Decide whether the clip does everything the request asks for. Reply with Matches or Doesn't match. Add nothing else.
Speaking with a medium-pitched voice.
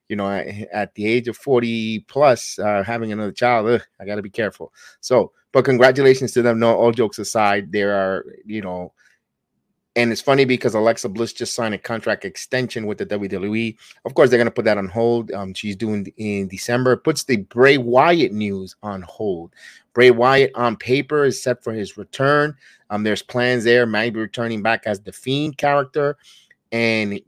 Doesn't match